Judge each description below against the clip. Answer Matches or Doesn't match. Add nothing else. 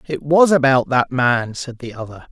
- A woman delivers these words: Doesn't match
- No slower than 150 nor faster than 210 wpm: Matches